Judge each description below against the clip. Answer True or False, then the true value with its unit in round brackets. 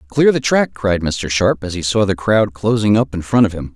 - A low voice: True (100 Hz)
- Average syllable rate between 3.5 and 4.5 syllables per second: False (5.1 syllables/s)